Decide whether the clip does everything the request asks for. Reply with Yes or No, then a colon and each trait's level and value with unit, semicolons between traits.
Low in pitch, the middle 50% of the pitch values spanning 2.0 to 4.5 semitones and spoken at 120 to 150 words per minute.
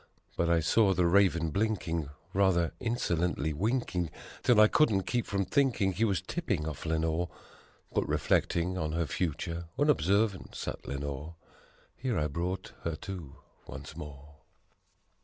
Yes: very low, 90 Hz; average, 3.9 semitones; average, 140 wpm